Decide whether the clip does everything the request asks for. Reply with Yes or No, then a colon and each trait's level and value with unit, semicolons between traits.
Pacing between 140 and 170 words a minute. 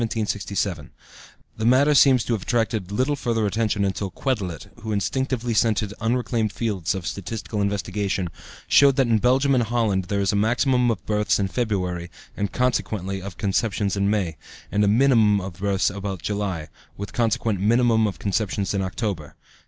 Yes: average, 160 wpm